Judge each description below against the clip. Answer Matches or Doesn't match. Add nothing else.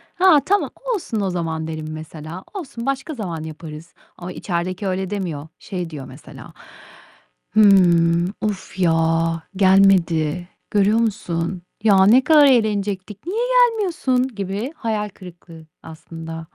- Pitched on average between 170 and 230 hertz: Matches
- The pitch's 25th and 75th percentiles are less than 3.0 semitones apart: Doesn't match